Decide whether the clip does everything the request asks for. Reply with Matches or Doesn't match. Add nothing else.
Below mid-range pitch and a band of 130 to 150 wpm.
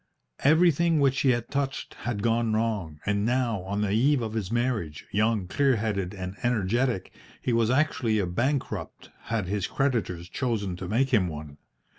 Doesn't match